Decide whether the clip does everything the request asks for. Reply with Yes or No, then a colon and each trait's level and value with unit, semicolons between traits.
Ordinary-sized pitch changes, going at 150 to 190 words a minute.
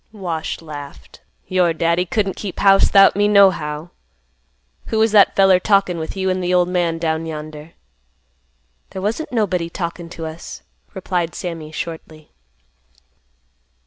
No: average, 3.3 semitones; average, 140 wpm